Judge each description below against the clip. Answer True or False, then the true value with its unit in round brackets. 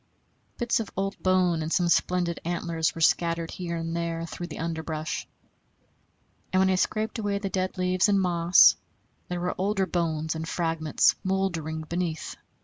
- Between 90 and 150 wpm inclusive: False (160 wpm)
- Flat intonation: True (2.3 semitones)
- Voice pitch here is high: False (175 Hz)